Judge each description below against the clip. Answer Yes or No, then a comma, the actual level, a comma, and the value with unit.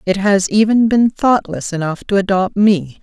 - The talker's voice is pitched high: Yes, high, 200 Hz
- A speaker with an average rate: Yes, average, 180 wpm